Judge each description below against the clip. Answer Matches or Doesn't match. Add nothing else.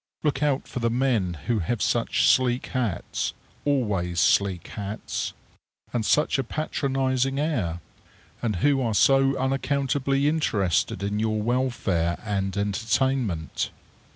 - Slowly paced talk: Matches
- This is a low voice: Matches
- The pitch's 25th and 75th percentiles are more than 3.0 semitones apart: Matches